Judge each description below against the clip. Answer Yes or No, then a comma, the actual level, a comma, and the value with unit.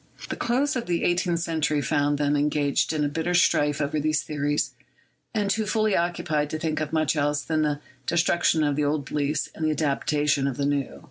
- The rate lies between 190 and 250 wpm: Yes, average, 200 wpm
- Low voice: No, medium, 155 Hz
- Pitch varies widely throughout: No, narrow, 2.5 semitones